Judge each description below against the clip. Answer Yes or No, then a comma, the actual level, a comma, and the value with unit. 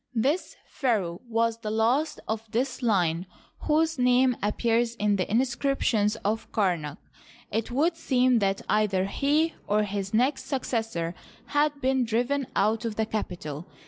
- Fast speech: No, average, 145 wpm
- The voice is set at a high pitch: Yes, high, 225 Hz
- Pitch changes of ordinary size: Yes, average, 4.1 semitones